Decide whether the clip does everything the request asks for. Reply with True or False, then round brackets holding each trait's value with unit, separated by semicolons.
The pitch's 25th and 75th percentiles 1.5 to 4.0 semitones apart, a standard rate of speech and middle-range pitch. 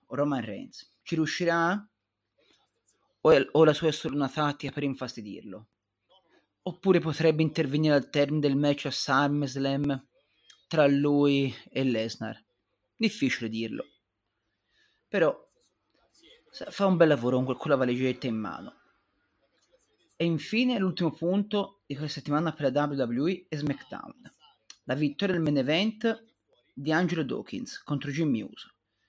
True (3.5 semitones; 125 wpm; 145 Hz)